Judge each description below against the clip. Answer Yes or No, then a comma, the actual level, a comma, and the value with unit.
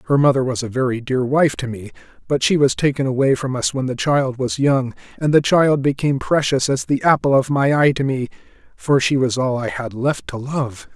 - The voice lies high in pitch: No, low, 130 Hz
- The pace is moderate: No, fast, 235 wpm